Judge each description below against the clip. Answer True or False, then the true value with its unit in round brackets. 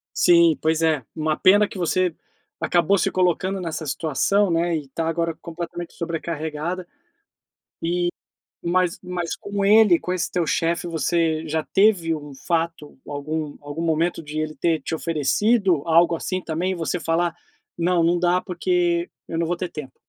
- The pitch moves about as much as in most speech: False (1.9 semitones)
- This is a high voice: False (170 Hz)